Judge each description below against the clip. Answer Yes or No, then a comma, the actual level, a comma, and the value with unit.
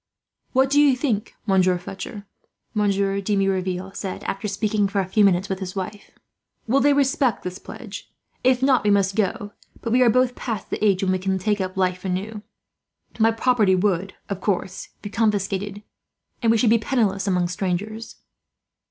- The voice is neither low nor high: No, high, 200 Hz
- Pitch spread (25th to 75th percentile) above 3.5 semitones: No, average, 3.0 semitones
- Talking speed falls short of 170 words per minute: No, average, 180 wpm